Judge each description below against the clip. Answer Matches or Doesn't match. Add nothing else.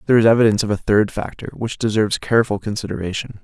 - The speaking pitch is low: Matches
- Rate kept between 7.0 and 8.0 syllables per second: Matches